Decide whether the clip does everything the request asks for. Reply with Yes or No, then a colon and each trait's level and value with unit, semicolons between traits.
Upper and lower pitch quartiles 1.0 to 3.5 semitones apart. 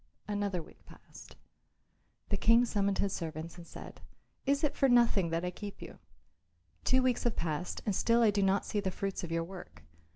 No: average, 4.8 semitones